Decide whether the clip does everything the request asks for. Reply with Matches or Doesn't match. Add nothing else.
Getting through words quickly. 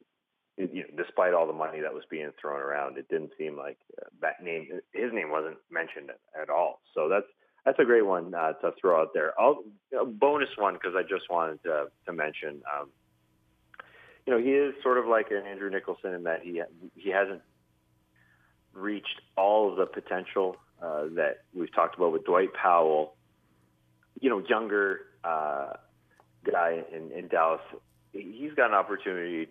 Doesn't match